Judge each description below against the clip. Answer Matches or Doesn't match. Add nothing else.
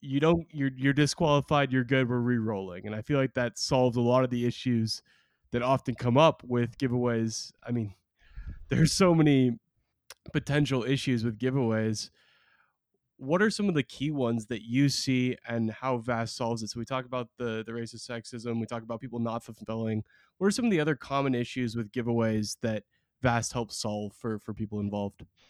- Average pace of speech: Matches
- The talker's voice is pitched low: Matches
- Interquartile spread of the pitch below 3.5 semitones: Matches